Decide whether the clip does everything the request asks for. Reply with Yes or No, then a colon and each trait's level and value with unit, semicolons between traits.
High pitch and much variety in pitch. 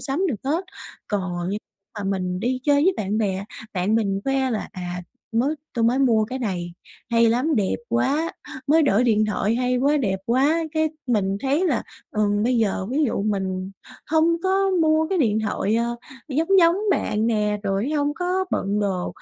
Yes: high, 235 Hz; wide, 6.3 semitones